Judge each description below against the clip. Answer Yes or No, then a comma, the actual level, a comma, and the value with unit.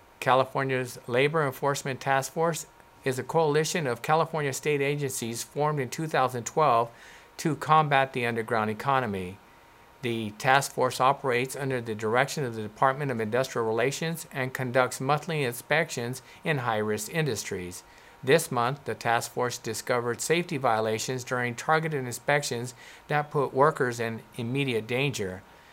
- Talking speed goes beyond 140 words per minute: No, slow, 135 wpm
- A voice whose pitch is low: Yes, low, 130 Hz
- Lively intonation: No, average, 3.8 semitones